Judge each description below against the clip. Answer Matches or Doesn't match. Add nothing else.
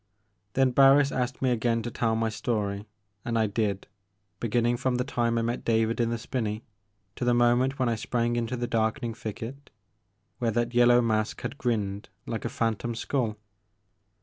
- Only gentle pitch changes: Matches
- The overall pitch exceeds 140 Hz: Doesn't match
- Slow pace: Doesn't match